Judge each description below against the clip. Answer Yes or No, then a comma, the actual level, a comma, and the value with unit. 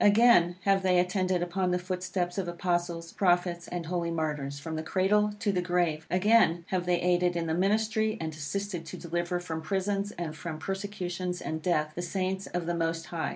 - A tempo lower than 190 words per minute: No, average, 195 wpm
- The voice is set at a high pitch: No, medium, 175 Hz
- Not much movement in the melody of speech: Yes, narrow, 2.1 semitones